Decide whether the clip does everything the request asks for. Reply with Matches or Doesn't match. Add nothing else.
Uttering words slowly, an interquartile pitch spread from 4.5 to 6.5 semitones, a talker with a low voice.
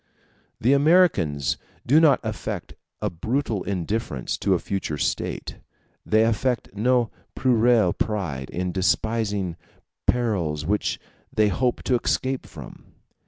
Matches